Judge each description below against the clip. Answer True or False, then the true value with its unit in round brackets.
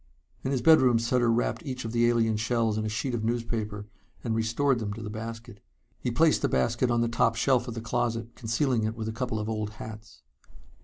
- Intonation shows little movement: True (1.6 semitones)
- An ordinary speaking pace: False (220 wpm)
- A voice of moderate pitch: False (115 Hz)